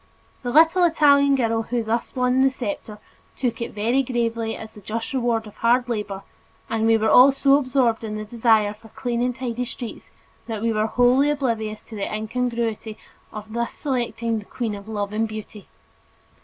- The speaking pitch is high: Yes, high, 230 Hz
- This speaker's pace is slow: No, average, 185 wpm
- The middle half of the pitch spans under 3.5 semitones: Yes, narrow, 2.5 semitones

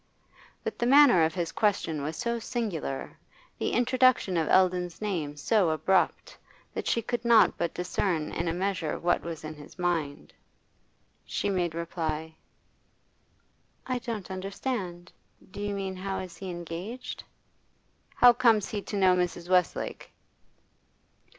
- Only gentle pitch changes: No, average, 4.1 semitones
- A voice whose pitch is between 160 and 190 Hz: Yes, medium, 185 Hz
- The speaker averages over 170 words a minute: No, average, 140 wpm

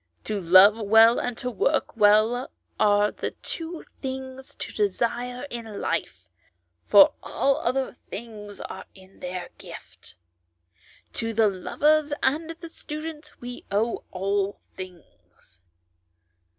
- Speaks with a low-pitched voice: No, high, 225 Hz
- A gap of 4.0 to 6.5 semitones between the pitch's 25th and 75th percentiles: Yes, average, 4.7 semitones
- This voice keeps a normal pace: No, slow, 120 wpm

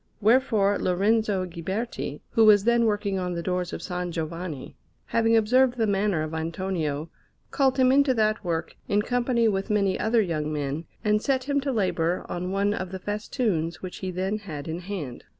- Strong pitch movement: No, average, 4.6 semitones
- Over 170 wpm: Yes, average, 185 wpm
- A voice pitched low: No, high, 195 Hz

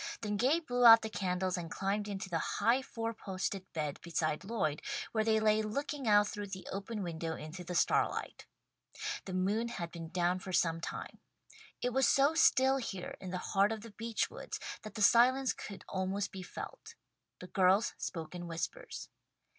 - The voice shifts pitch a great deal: No, average, 4.1 semitones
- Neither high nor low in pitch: No, high, 200 Hz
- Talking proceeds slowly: No, average, 185 wpm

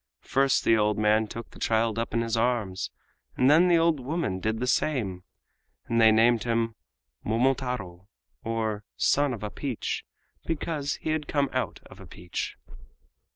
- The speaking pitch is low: Yes, low, 115 Hz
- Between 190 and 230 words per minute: No, average, 165 wpm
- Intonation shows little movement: No, average, 4.0 semitones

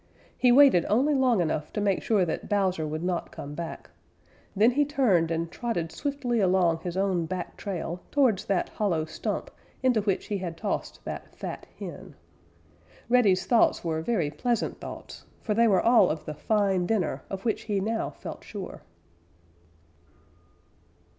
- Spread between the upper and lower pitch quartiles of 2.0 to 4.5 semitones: No, average, 5.3 semitones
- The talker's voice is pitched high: Yes, high, 195 Hz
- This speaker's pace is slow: No, average, 160 wpm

